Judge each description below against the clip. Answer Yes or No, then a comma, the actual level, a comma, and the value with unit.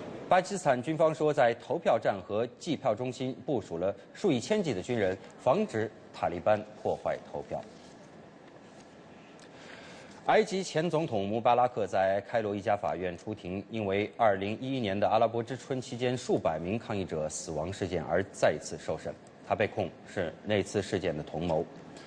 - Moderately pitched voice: No, low, 115 Hz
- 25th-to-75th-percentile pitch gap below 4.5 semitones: No, average, 5.1 semitones